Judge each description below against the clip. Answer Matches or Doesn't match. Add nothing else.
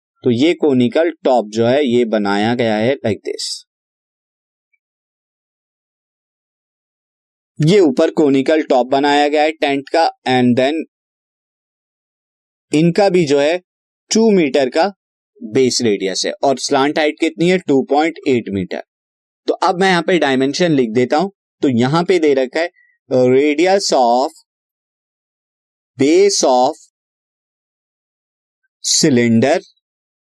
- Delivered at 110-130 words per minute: Matches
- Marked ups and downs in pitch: Matches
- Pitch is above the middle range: Doesn't match